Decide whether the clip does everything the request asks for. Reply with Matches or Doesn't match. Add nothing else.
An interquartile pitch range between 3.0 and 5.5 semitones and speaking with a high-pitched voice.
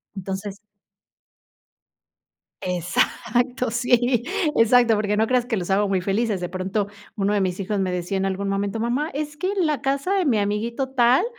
Matches